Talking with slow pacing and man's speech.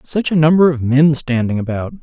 No: fast, 205 wpm; male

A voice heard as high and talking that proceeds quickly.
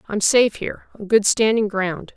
No: high, 210 Hz; average, 195 wpm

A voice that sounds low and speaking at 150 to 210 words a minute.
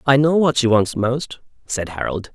Yes: low, 125 Hz; fast, 205 wpm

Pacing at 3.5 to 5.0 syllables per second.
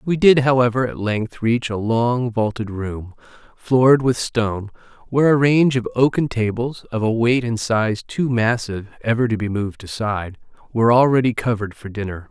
No: 5.2 syllables/s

